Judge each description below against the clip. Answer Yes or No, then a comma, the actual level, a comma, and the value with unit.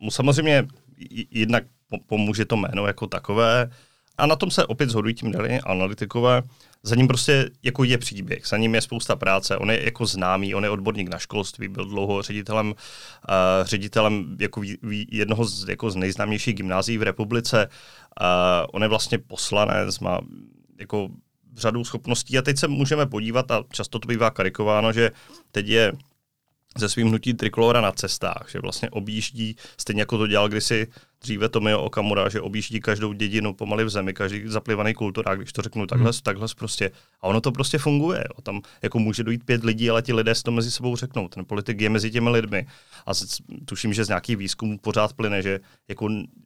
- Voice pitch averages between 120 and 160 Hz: No, low, 110 Hz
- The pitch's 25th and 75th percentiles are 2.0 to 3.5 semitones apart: Yes, narrow, 2.5 semitones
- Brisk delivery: Yes, fast, 185 wpm